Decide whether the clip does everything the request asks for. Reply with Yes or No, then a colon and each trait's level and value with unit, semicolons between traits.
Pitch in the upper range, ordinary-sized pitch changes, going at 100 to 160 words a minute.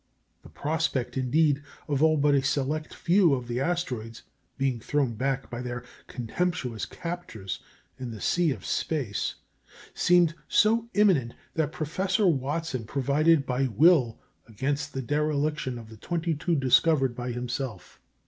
No: medium, 140 Hz; average, 4.7 semitones; average, 140 wpm